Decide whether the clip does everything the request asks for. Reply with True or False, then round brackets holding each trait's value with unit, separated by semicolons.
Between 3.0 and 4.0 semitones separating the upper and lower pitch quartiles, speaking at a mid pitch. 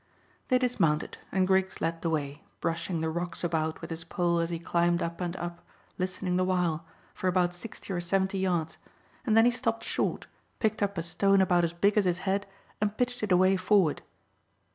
False (2.5 semitones; 180 Hz)